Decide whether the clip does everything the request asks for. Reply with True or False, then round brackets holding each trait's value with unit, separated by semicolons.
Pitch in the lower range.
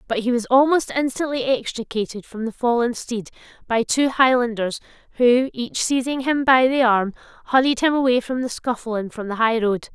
False (245 Hz)